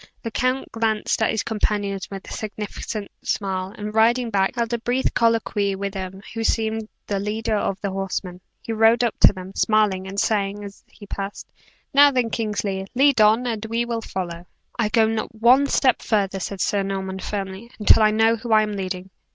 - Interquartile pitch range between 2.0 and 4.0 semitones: Yes, narrow, 2.5 semitones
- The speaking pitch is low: No, high, 215 Hz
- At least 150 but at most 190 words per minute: No, average, 200 wpm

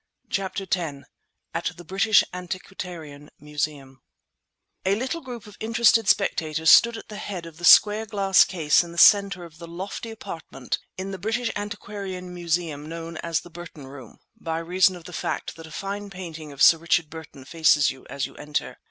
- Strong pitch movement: No, average, 3.8 semitones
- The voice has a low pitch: No, medium, 175 Hz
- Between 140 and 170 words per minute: No, average, 180 wpm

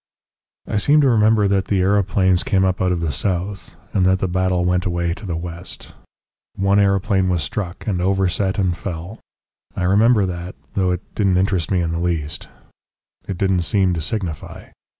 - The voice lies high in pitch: No, very low, 95 Hz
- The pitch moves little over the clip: Yes, narrow, 2.0 semitones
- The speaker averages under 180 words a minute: No, average, 185 wpm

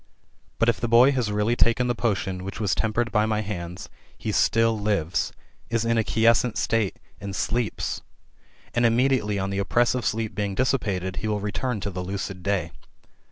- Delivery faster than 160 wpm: Yes, average, 180 wpm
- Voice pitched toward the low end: Yes, low, 110 Hz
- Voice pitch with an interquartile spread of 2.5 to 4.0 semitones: Yes, average, 3.0 semitones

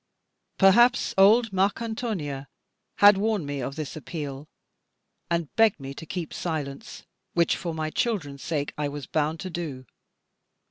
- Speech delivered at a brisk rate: No, average, 140 wpm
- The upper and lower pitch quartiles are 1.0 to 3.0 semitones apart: No, wide, 5.5 semitones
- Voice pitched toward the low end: No, medium, 165 Hz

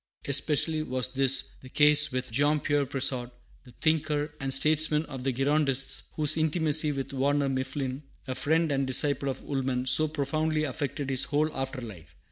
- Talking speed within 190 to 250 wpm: No, average, 165 wpm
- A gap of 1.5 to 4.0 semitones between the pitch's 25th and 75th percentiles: Yes, narrow, 2.5 semitones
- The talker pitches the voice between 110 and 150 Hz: Yes, medium, 140 Hz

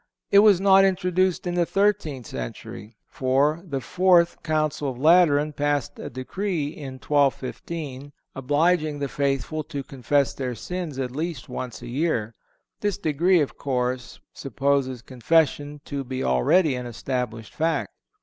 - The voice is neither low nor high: Yes, medium, 145 Hz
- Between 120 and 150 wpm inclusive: Yes, average, 140 wpm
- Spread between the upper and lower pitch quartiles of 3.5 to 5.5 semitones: Yes, average, 4.6 semitones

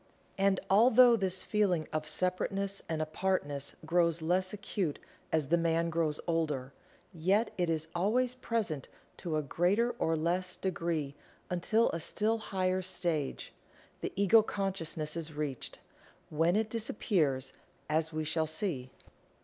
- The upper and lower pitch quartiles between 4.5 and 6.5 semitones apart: No, average, 4.0 semitones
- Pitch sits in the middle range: Yes, medium, 175 Hz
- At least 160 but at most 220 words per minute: No, slow, 135 wpm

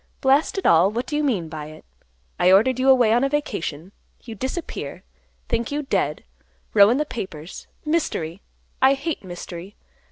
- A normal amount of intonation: No, wide, 7.6 semitones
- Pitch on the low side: No, high, 230 Hz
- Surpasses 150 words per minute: Yes, average, 170 wpm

